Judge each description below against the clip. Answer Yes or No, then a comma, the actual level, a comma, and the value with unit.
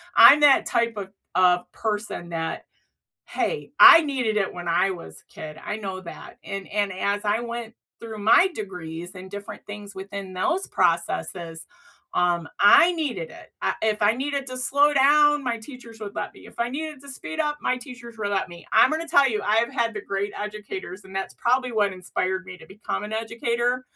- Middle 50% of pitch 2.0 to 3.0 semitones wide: No, average, 4.8 semitones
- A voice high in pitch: Yes, high, 215 Hz